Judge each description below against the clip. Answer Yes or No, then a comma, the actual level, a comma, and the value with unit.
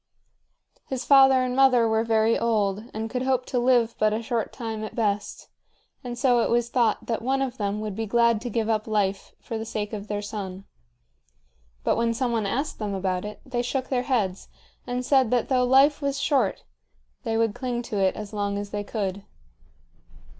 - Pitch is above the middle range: Yes, high, 230 Hz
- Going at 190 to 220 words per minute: Yes, fast, 205 wpm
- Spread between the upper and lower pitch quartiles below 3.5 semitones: Yes, average, 3.0 semitones